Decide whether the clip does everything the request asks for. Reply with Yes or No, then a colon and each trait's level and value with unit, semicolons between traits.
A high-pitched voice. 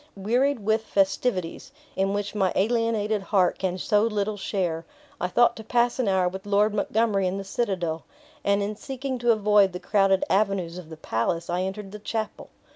Yes: high, 200 Hz